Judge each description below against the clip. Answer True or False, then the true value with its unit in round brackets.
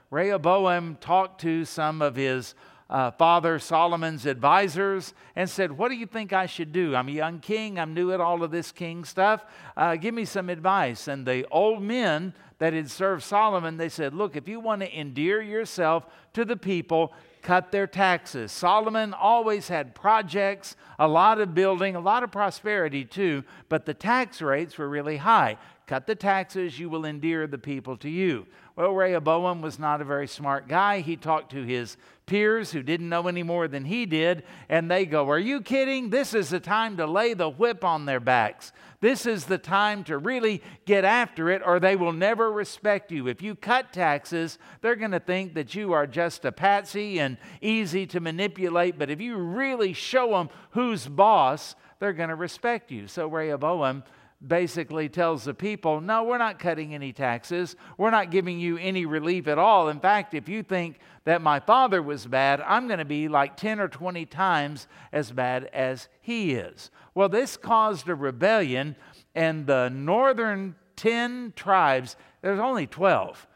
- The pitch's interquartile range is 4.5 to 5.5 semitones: True (4.8 semitones)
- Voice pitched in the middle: True (175 Hz)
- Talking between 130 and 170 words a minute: False (190 wpm)